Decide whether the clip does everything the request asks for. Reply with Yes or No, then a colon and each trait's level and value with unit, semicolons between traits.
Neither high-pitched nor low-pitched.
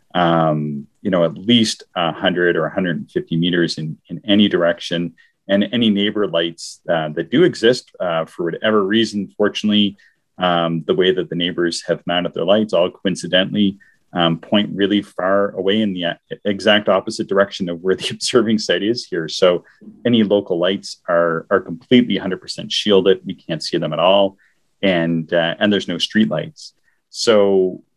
No: very low, 95 Hz